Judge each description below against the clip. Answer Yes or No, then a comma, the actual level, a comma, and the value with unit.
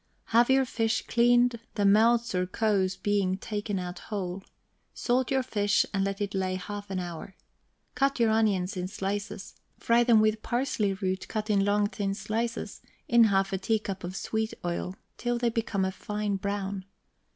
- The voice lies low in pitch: No, high, 205 Hz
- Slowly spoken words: No, average, 175 wpm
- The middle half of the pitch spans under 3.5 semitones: Yes, average, 2.9 semitones